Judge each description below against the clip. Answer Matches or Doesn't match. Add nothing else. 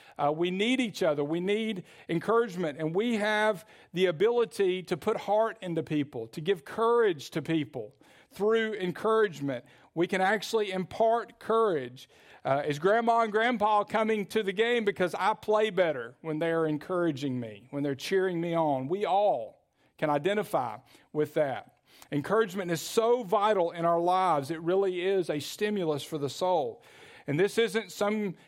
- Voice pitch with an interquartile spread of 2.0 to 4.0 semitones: Doesn't match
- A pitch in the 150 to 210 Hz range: Matches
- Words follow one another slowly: Doesn't match